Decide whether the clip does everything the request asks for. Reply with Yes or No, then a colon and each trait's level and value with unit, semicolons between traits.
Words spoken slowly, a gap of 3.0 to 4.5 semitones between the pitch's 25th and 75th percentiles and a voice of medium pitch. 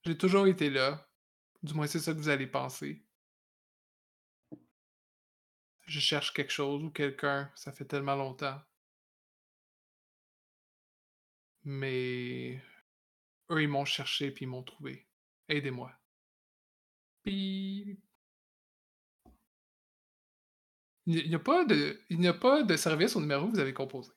Yes: slow, 115 wpm; average, 3.9 semitones; medium, 145 Hz